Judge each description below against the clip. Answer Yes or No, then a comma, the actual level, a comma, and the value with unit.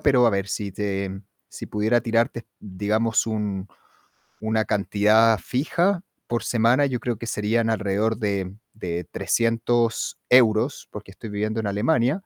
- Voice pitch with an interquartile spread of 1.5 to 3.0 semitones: Yes, narrow, 2.4 semitones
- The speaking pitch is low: Yes, low, 110 Hz